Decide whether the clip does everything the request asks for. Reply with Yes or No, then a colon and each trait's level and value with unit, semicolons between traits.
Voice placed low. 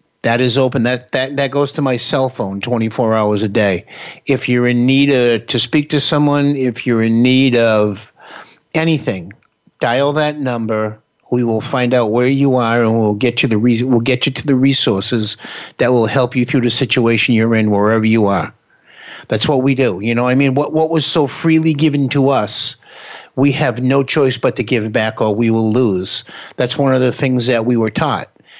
Yes: low, 125 Hz